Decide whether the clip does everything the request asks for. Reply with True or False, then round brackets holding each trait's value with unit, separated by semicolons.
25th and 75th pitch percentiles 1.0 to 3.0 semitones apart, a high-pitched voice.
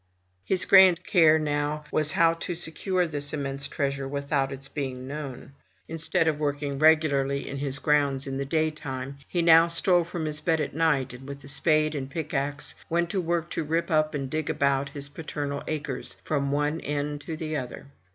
False (2.4 semitones; 150 Hz)